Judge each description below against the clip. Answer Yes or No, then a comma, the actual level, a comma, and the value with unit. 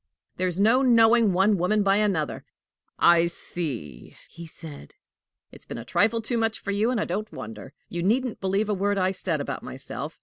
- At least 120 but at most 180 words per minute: No, average, 190 wpm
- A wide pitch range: No, average, 4.2 semitones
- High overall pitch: Yes, high, 195 Hz